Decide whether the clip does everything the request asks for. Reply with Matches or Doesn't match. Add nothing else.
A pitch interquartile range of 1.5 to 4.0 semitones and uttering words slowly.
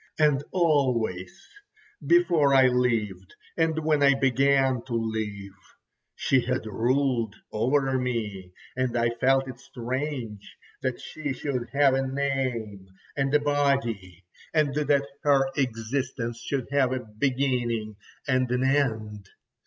Matches